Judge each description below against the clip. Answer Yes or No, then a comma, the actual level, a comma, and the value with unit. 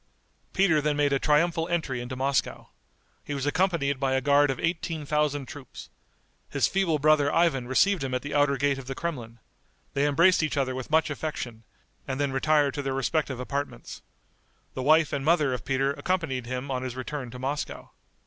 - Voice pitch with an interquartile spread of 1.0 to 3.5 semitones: Yes, narrow, 2.6 semitones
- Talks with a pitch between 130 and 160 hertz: Yes, medium, 140 Hz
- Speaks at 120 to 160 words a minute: No, average, 190 wpm